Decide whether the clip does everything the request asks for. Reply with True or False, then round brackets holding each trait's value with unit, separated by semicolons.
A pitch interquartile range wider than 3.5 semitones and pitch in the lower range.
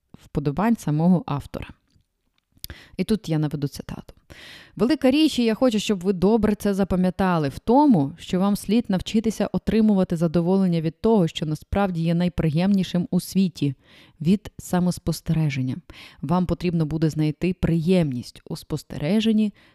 False (4.2 semitones; 180 Hz)